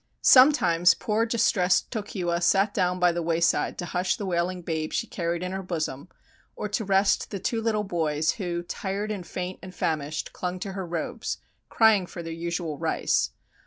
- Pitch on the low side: No, medium, 180 Hz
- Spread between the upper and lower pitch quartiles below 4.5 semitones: Yes, average, 2.8 semitones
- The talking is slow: No, average, 180 wpm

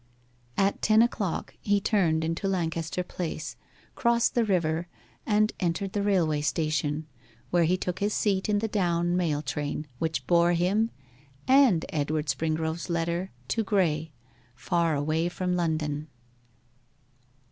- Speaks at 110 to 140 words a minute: Yes, slow, 135 wpm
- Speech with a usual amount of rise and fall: Yes, average, 3.7 semitones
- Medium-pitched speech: Yes, medium, 170 Hz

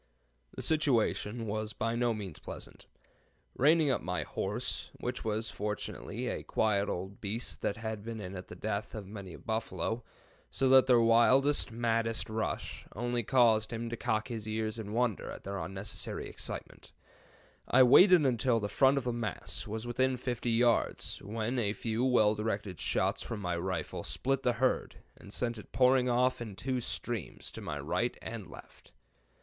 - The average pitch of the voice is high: No, low, 115 Hz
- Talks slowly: No, average, 175 wpm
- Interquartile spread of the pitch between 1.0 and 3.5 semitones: Yes, average, 2.7 semitones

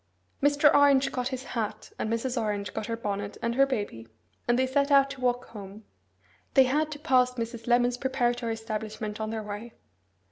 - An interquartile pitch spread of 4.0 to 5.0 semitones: No, average, 3.3 semitones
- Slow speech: No, average, 185 wpm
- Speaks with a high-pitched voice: Yes, high, 240 Hz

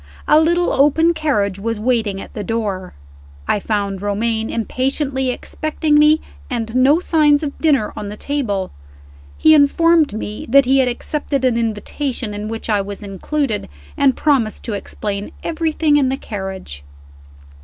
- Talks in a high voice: Yes, very high, 250 Hz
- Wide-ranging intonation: Yes, wide, 6.0 semitones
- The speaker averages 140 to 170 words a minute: Yes, average, 155 wpm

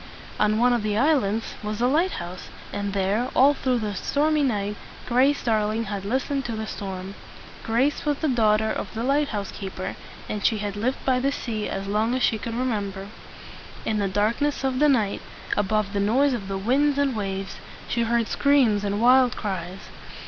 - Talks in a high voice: Yes, high, 220 Hz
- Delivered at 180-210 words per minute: Yes, average, 200 wpm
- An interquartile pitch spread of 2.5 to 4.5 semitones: Yes, average, 4.2 semitones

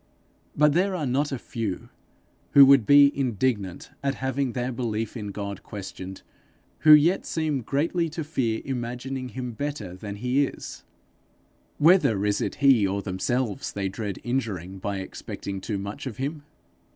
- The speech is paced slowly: No, average, 155 wpm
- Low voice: Yes, low, 125 Hz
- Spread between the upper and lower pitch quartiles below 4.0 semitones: No, wide, 5.6 semitones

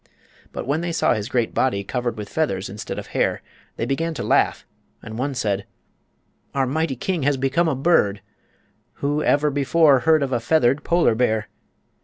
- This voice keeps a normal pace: Yes, average, 180 wpm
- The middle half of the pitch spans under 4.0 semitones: No, average, 5.2 semitones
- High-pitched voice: No, low, 135 Hz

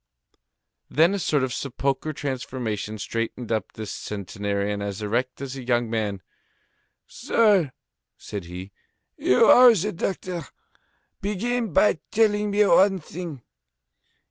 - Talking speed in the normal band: No, slow, 120 wpm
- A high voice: No, low, 130 Hz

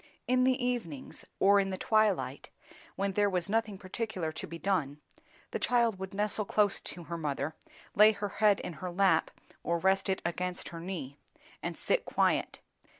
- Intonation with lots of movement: No, average, 3.7 semitones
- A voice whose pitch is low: No, high, 190 Hz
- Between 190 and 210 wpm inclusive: No, average, 175 wpm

